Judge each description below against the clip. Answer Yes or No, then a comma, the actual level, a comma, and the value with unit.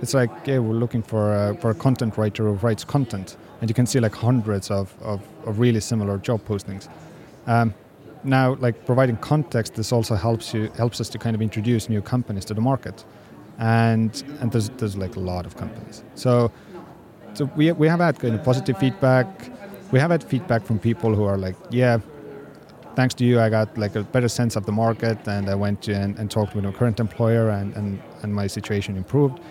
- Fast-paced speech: Yes, fast, 215 wpm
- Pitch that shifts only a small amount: No, average, 3.0 semitones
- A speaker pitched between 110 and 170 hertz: Yes, low, 115 Hz